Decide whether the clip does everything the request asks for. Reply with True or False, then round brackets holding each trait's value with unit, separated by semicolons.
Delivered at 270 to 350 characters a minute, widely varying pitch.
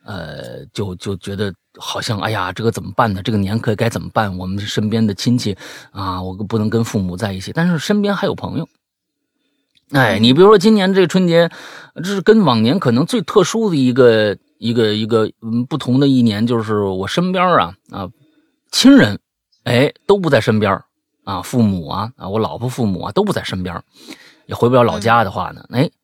True (280 characters per minute; 7.4 semitones)